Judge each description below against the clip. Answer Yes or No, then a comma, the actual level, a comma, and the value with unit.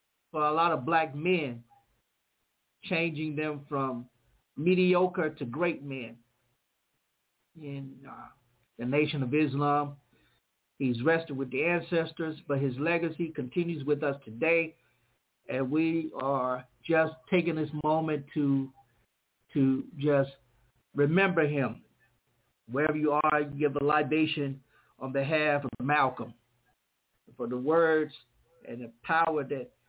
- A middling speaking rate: No, slow, 120 wpm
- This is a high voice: No, medium, 145 Hz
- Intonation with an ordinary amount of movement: Yes, average, 3.5 semitones